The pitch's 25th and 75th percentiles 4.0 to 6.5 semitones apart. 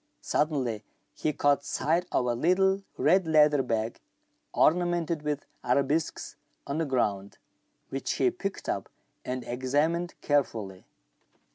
Yes: average, 4.7 semitones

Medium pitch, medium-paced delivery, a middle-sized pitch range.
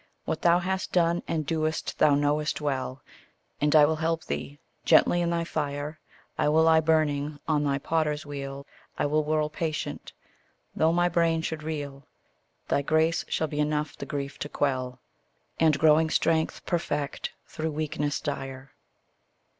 No: medium, 155 Hz; average, 155 wpm; narrow, 1.9 semitones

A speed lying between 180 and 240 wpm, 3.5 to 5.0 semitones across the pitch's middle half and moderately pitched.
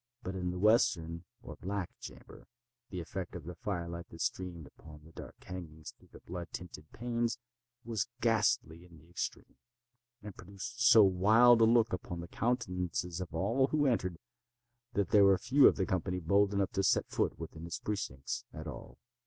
No: average, 185 wpm; average, 4.1 semitones; very low, 90 Hz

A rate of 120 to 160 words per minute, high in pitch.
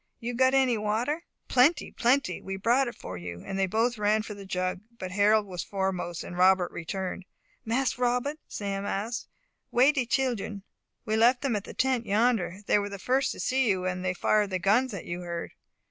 No: fast, 205 wpm; high, 210 Hz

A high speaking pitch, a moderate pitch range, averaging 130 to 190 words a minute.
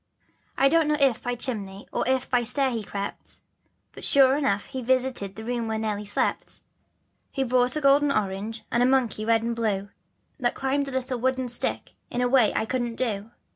No: high, 245 Hz; average, 3.1 semitones; average, 200 wpm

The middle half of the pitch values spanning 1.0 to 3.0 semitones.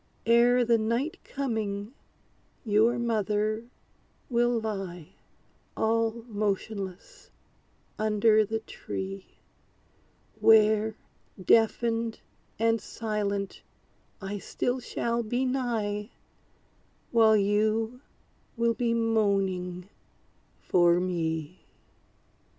Yes: narrow, 2.5 semitones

